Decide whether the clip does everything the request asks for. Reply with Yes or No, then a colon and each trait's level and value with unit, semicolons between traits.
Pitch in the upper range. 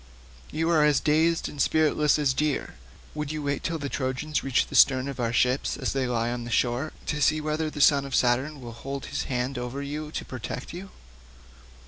No: medium, 140 Hz